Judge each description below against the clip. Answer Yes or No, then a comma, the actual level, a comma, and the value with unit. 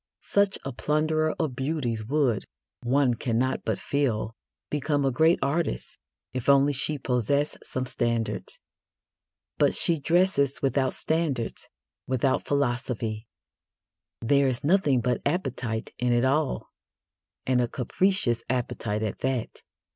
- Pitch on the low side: Yes, low, 130 Hz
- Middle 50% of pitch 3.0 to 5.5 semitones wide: Yes, average, 3.6 semitones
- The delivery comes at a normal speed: No, slow, 125 wpm